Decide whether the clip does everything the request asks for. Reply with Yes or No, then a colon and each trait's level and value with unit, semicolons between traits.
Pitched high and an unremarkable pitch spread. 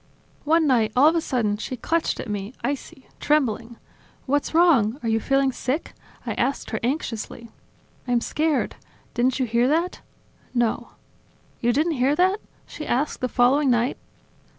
Yes: very high, 260 Hz; average, 4.2 semitones